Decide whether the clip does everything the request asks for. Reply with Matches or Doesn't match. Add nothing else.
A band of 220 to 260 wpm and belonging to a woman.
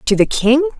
Matches